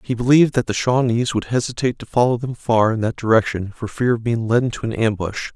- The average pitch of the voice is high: No, low, 115 Hz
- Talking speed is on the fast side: Yes, fast, 240 wpm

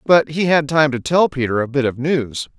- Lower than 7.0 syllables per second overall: Yes, 5.0 syllables/s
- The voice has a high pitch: No, medium, 140 Hz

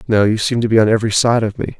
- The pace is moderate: No, fast, 335 wpm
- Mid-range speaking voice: No, low, 110 Hz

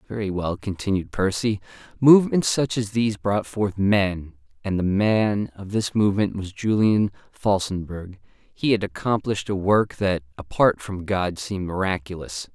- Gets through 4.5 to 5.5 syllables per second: Yes, 4.6 syllables/s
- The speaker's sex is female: No, male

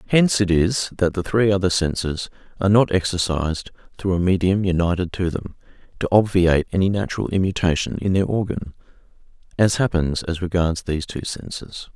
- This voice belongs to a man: Yes, male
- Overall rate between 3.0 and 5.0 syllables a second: No, 5.6 syllables/s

